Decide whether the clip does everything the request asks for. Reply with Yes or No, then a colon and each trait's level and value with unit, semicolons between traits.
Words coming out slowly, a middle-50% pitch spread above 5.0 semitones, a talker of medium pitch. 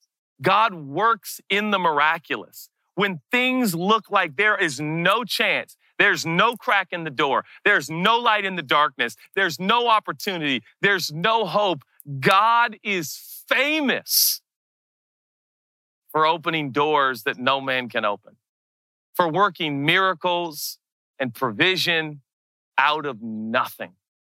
Yes: slow, 125 wpm; wide, 5.6 semitones; medium, 180 Hz